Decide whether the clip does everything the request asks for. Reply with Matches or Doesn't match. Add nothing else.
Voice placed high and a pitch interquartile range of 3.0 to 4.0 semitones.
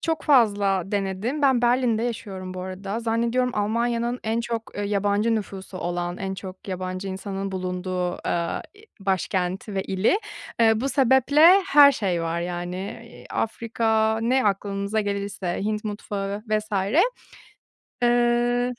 Matches